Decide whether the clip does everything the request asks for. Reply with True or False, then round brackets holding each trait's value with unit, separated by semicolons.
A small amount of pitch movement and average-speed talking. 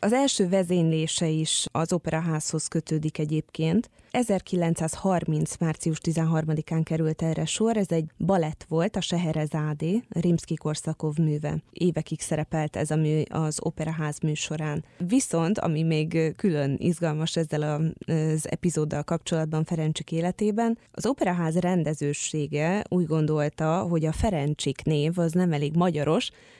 True (2.1 semitones; 125 wpm)